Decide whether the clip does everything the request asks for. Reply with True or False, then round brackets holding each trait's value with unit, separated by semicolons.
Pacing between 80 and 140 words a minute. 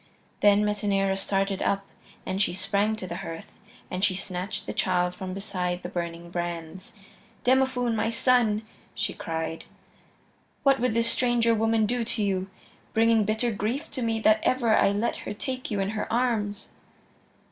False (165 wpm)